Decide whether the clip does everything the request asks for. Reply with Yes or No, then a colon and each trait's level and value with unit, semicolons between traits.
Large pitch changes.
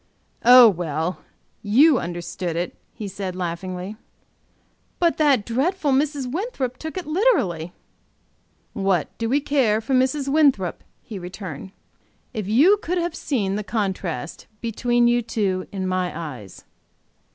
Yes: wide, 7.0 semitones